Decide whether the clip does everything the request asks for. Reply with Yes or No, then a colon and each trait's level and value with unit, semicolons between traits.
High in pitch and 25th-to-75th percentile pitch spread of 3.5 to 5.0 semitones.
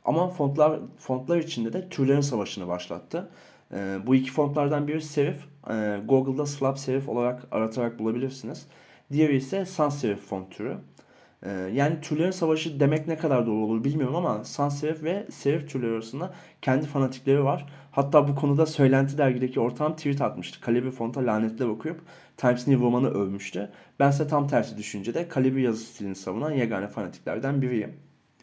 No: low, 135 Hz; average, 4.2 semitones